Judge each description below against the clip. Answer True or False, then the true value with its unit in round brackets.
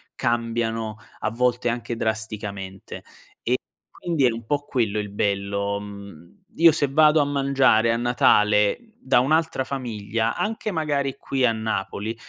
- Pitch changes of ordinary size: True (4.7 semitones)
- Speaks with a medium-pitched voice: False (115 Hz)